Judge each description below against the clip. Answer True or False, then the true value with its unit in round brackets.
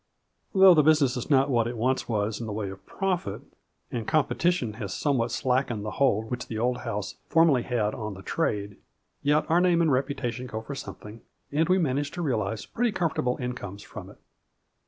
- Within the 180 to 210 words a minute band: True (200 wpm)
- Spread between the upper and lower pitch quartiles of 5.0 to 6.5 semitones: True (5.5 semitones)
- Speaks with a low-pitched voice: True (125 Hz)